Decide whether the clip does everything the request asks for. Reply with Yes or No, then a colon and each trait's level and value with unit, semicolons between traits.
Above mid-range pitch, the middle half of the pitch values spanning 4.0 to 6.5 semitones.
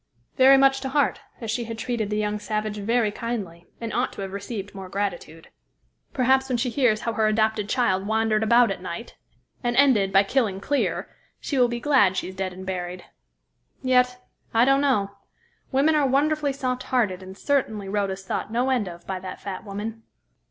Yes: high, 220 Hz; average, 4.5 semitones